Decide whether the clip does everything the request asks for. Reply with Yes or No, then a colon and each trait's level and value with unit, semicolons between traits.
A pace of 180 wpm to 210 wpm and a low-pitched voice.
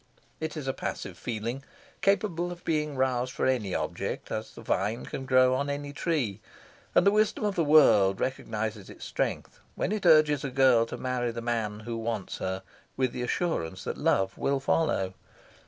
Yes: average, 185 wpm; low, 130 Hz